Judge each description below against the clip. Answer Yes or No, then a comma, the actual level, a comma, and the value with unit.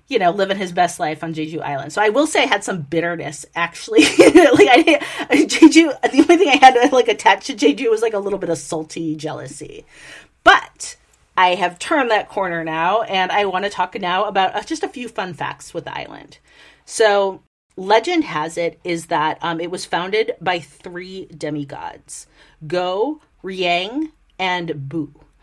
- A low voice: No, medium, 185 Hz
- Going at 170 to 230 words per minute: Yes, average, 190 wpm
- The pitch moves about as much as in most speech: No, wide, 6.0 semitones